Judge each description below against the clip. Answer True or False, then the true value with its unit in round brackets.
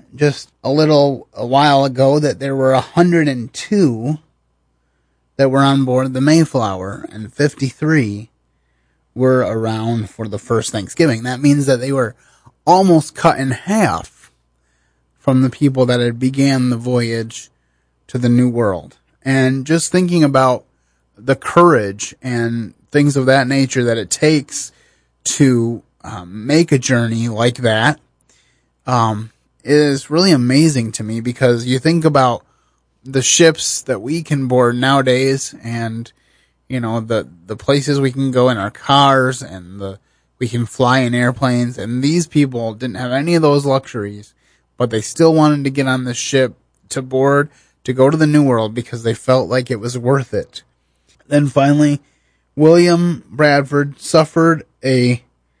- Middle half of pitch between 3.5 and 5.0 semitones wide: True (3.9 semitones)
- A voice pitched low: True (130 Hz)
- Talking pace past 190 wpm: False (155 wpm)